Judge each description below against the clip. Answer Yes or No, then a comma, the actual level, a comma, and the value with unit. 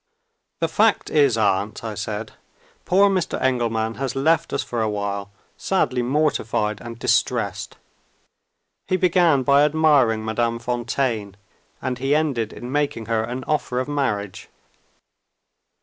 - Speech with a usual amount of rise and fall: Yes, average, 4.9 semitones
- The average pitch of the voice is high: No, low, 125 Hz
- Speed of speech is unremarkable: No, slow, 130 wpm